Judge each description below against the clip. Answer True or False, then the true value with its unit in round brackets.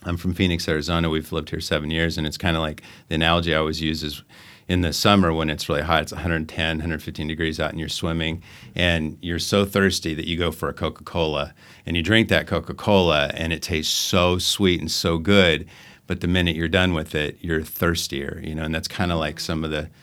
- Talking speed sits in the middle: False (235 wpm)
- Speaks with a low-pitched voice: True (80 Hz)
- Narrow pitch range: True (2.1 semitones)